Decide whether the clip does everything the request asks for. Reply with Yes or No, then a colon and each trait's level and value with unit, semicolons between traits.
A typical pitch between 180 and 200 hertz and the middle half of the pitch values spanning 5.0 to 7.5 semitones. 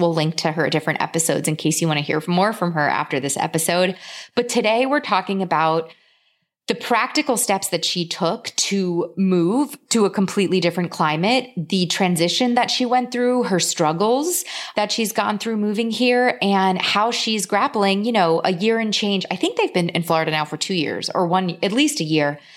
Yes: high, 190 Hz; wide, 5.4 semitones